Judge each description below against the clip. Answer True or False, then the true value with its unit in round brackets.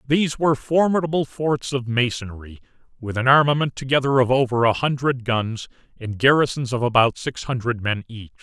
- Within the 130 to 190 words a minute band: True (165 wpm)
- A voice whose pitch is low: True (130 Hz)